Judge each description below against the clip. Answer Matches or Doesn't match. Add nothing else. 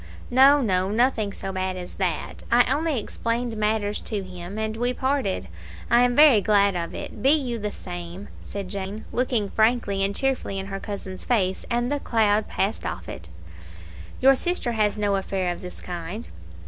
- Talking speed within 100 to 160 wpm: Doesn't match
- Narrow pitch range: Doesn't match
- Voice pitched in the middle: Doesn't match